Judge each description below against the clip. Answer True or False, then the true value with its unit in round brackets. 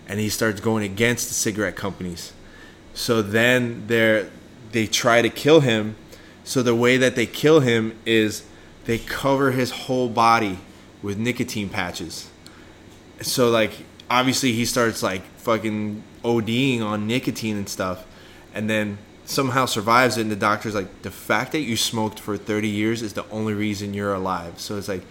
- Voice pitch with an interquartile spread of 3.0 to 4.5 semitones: False (2.5 semitones)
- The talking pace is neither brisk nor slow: True (165 wpm)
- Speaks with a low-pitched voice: True (110 Hz)